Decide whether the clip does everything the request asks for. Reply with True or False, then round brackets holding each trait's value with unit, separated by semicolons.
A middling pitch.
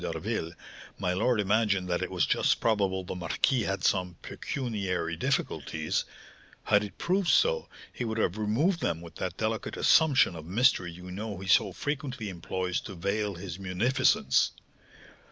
False (100 Hz)